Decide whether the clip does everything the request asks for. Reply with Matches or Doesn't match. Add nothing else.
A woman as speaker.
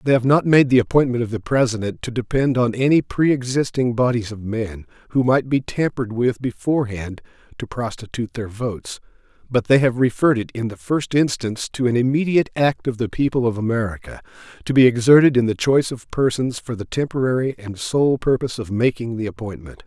Doesn't match